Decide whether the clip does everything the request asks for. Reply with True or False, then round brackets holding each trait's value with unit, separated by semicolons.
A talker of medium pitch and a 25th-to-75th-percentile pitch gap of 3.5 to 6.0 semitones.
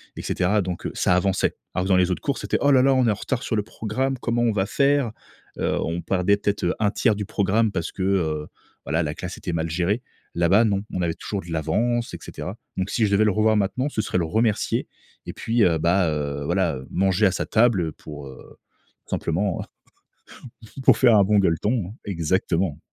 False (95 Hz; 4.2 semitones)